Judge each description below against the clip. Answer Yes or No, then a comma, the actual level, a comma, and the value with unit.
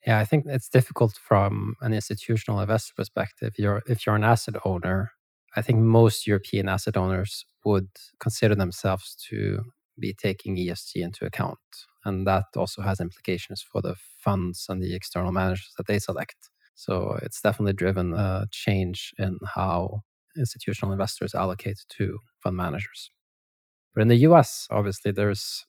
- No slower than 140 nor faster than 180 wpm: Yes, average, 155 wpm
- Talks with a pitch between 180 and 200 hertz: No, low, 100 Hz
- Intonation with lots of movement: No, average, 2.7 semitones